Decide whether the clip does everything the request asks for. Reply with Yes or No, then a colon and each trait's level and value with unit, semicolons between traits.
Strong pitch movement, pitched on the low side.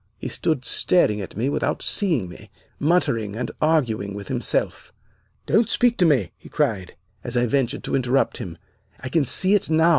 Yes: wide, 6.9 semitones; low, 130 Hz